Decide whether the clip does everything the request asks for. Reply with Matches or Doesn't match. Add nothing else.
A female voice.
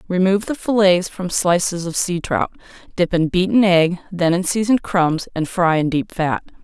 Matches